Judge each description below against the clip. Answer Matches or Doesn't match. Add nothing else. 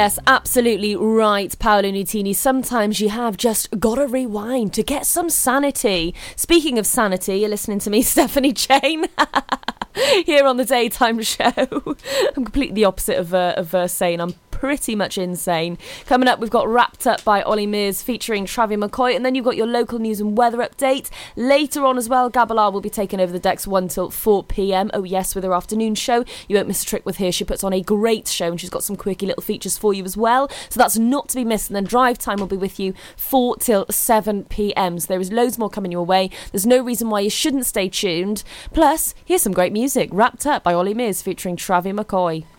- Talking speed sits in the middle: Doesn't match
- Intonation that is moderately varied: Matches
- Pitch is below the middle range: Doesn't match